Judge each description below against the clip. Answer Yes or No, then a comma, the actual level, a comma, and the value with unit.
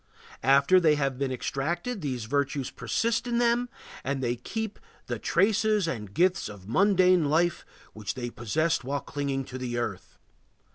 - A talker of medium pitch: Yes, medium, 145 Hz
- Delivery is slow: No, average, 155 wpm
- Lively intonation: Yes, wide, 6.6 semitones